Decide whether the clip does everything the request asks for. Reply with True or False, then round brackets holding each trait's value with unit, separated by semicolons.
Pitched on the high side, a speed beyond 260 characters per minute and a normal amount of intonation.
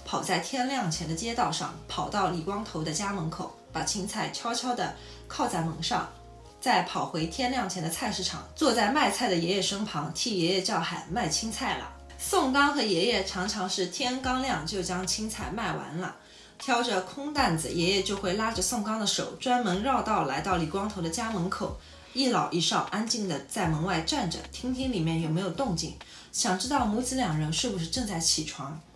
False (195 Hz; 285 characters per minute; 5.8 semitones)